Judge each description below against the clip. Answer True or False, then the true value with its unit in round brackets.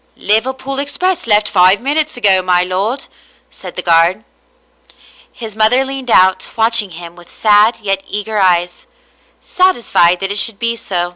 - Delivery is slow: False (150 wpm)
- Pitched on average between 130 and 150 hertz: False (210 Hz)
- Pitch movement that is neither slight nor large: True (4.8 semitones)